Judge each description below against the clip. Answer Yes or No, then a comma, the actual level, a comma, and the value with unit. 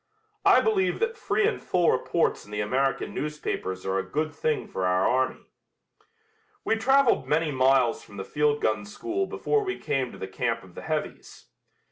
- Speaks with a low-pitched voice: No, medium, 145 Hz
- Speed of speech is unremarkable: Yes, average, 180 wpm